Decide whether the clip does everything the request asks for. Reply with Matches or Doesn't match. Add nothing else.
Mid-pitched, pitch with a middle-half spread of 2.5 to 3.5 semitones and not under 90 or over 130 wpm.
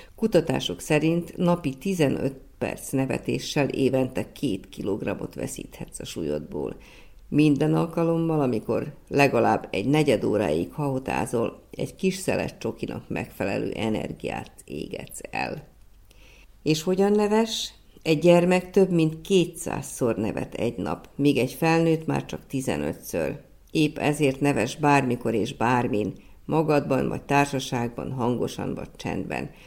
Doesn't match